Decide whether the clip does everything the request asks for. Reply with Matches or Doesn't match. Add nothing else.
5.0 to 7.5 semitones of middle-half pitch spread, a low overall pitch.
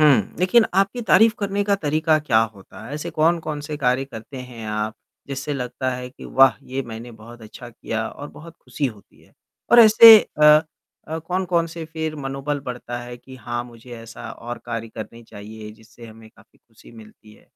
Matches